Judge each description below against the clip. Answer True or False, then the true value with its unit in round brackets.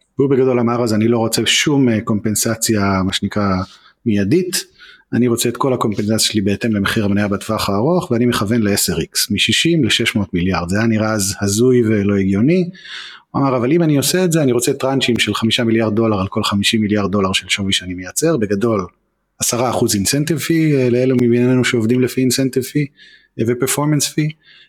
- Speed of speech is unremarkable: False (170 wpm)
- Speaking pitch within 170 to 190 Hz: False (115 Hz)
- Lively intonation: False (4.0 semitones)